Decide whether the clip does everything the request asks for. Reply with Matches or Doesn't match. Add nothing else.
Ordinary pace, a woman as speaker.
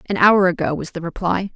Doesn't match